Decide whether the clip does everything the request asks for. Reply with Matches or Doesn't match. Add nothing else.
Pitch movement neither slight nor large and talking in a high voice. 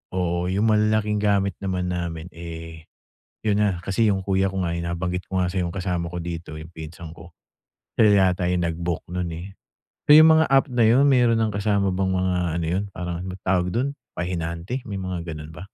Doesn't match